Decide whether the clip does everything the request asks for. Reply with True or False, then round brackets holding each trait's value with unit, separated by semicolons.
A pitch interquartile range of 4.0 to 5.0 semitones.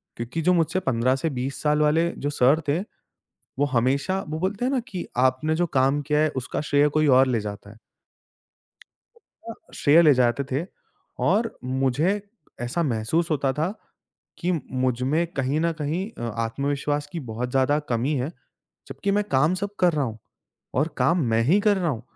True (4.7 semitones)